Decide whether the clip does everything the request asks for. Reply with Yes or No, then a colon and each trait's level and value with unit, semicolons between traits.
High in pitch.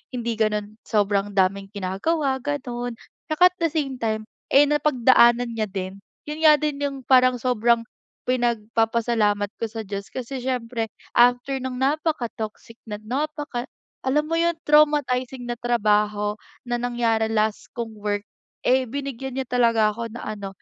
Yes: high, 240 Hz